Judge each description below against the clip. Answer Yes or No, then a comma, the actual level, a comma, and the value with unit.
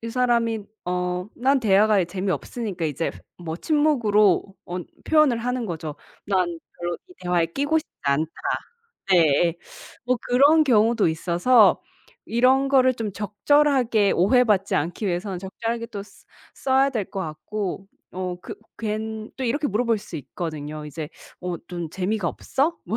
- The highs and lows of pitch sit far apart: Yes, wide, 5.8 semitones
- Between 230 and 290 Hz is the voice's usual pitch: No, high, 210 Hz